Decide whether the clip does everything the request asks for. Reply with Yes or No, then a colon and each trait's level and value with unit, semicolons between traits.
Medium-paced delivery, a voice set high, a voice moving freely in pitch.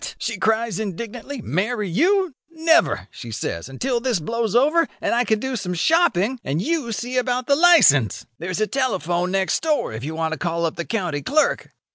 Yes: average, 190 wpm; high, 225 Hz; wide, 7.4 semitones